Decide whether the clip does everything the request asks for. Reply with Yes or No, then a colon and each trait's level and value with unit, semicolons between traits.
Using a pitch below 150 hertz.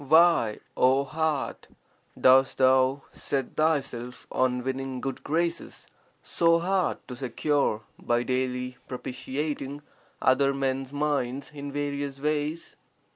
Yes: low, 135 Hz